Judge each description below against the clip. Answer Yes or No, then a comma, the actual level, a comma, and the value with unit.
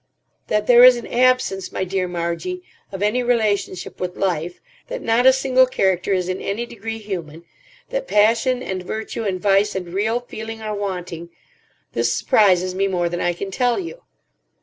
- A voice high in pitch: Yes, high, 205 Hz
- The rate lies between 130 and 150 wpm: No, average, 170 wpm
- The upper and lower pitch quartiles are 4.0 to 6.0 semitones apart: Yes, average, 4.6 semitones